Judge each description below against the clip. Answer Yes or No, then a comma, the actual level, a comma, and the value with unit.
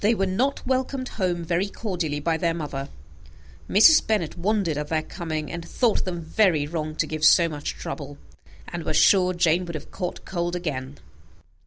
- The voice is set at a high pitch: No, medium, 170 Hz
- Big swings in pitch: No, average, 3.6 semitones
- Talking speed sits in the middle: Yes, average, 180 wpm